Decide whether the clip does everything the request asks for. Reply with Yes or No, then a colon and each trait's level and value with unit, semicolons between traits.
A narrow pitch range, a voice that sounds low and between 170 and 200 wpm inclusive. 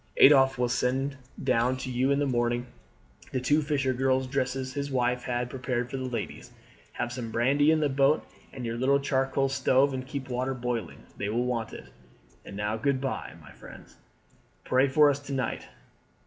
Yes: narrow, 1.9 semitones; low, 130 Hz; average, 190 wpm